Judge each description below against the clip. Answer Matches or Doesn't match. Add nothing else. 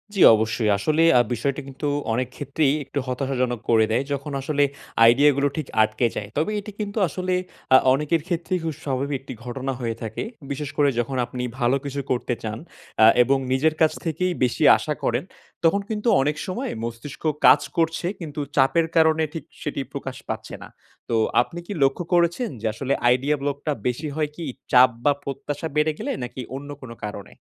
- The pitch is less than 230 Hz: Matches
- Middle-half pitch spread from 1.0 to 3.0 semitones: Doesn't match